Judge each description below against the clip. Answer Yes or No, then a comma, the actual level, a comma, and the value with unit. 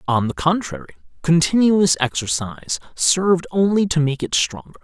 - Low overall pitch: No, medium, 155 Hz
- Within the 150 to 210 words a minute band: No, slow, 135 wpm